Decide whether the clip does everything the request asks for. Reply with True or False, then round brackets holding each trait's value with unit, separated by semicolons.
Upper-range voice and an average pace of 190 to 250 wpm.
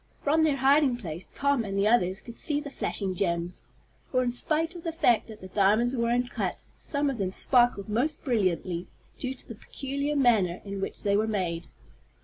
True (235 Hz; 195 wpm)